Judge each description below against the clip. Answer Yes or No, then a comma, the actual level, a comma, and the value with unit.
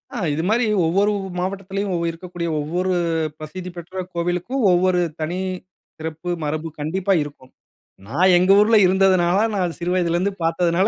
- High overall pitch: No, medium, 180 Hz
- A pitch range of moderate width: No, narrow, 2.2 semitones